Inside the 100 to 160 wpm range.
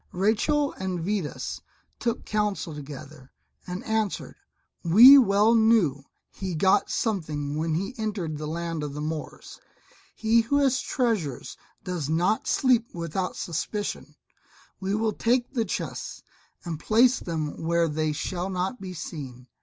Yes: average, 140 wpm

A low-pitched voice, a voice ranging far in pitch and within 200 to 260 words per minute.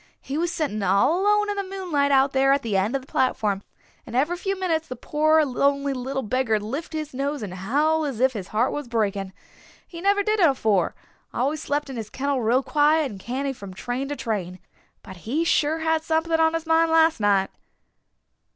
No: very high, 275 Hz; wide, 5.9 semitones; fast, 205 wpm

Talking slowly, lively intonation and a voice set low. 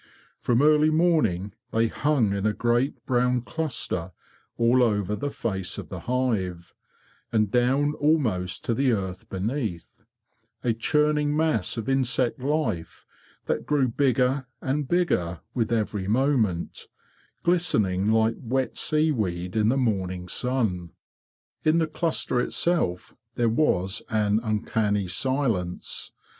Yes: slow, 125 wpm; wide, 5.8 semitones; low, 120 Hz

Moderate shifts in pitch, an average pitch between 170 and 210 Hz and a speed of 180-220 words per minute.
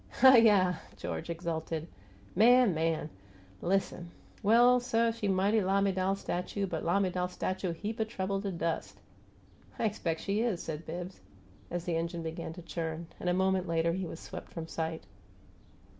No: average, 3.2 semitones; medium, 185 Hz; average, 155 wpm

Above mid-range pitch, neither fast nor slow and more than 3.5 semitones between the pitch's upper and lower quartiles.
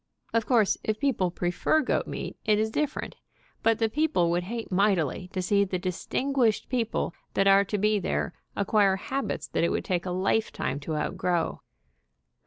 Yes: high, 200 Hz; average, 180 wpm; average, 3.9 semitones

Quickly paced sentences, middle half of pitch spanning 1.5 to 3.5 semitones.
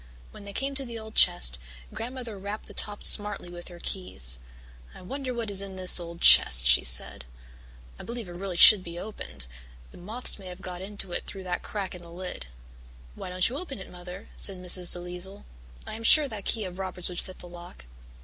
Yes: fast, 215 wpm; average, 3.1 semitones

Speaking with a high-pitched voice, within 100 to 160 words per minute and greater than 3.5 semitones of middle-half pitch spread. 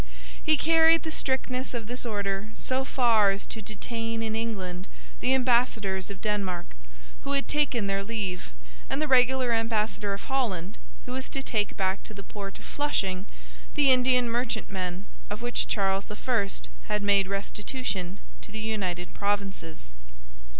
Yes: high, 215 Hz; average, 155 wpm; average, 4.2 semitones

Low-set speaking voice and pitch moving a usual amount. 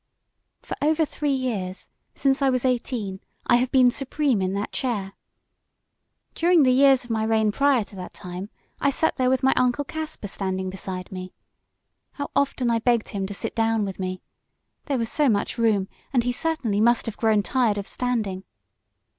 No: high, 235 Hz; average, 4.9 semitones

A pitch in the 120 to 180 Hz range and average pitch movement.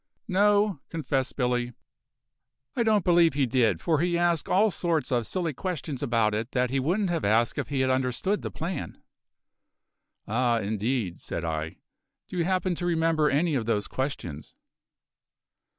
No: medium, 140 Hz; wide, 6.6 semitones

